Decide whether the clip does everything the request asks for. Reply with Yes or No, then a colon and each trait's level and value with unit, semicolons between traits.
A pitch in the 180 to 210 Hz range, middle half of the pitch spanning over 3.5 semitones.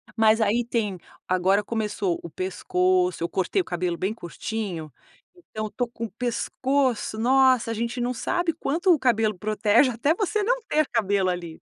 No: high, 220 Hz; wide, 5.4 semitones